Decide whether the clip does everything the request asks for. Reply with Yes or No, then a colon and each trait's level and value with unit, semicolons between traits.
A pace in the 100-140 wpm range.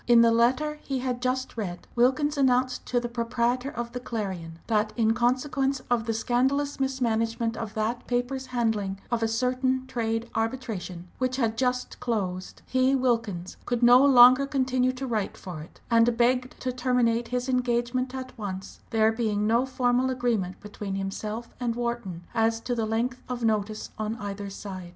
No: average, 170 wpm